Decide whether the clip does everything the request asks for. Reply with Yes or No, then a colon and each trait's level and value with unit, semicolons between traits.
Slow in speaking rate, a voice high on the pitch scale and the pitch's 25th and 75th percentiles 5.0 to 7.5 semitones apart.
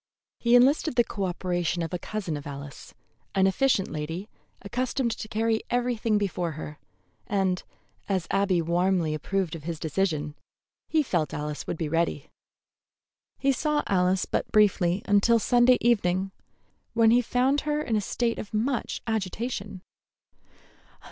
No: average, 145 wpm; high, 195 Hz; wide, 5.4 semitones